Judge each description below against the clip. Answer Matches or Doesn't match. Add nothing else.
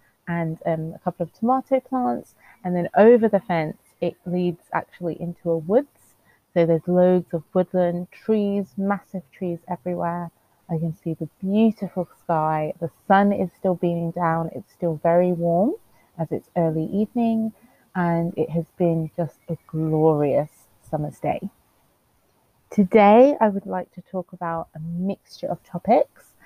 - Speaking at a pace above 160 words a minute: Doesn't match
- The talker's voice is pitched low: Doesn't match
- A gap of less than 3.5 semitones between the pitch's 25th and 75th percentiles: Matches